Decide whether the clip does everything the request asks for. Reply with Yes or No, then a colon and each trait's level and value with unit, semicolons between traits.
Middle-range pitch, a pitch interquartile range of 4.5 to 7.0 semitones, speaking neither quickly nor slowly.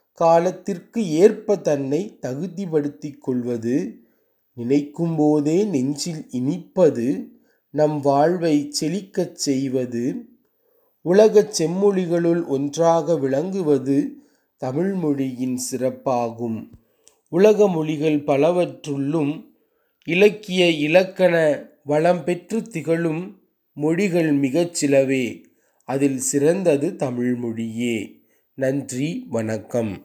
No: medium, 155 Hz; average, 4.9 semitones; slow, 70 wpm